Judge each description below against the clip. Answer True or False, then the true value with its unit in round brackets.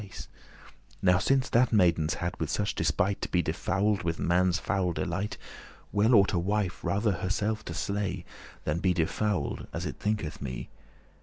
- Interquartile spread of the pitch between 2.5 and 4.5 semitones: True (3.2 semitones)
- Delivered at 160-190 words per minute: True (165 wpm)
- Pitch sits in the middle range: False (95 Hz)